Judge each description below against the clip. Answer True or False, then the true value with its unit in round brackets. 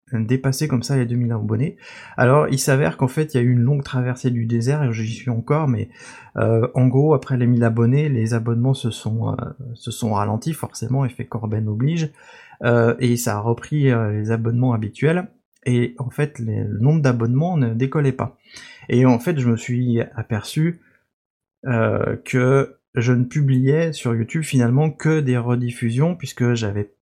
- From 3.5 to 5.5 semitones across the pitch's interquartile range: False (2.8 semitones)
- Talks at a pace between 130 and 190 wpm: True (185 wpm)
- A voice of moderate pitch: False (125 Hz)